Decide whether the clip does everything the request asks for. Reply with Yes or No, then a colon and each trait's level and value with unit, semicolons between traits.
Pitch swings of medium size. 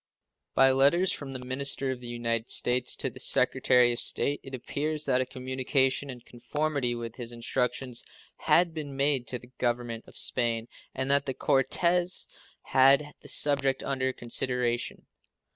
No: narrow, 2.3 semitones